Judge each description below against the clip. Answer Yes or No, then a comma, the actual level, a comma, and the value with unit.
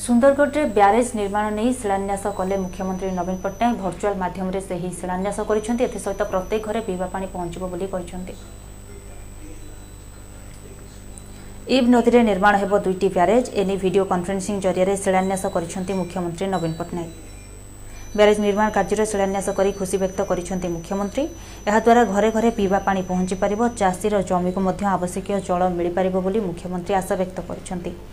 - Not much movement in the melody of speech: Yes, narrow, 2.2 semitones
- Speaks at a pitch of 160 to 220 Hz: Yes, high, 190 Hz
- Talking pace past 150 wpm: No, average, 115 wpm